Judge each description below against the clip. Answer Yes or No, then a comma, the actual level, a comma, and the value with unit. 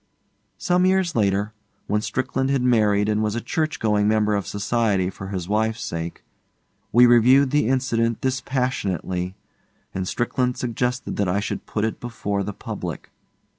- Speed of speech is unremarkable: Yes, average, 155 wpm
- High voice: No, low, 110 Hz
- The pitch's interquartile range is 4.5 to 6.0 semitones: No, average, 3.7 semitones